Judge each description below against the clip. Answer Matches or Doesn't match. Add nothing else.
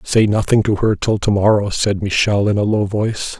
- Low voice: Matches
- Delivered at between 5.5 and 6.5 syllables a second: Doesn't match